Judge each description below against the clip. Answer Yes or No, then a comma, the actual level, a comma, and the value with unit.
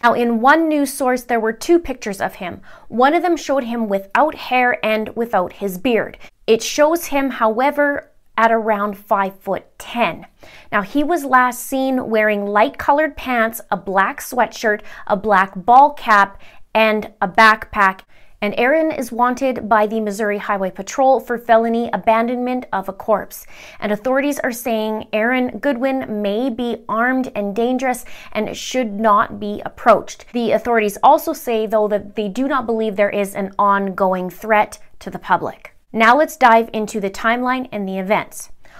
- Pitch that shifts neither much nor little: Yes, average, 3.6 semitones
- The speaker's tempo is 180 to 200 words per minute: No, average, 165 wpm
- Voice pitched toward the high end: Yes, high, 225 Hz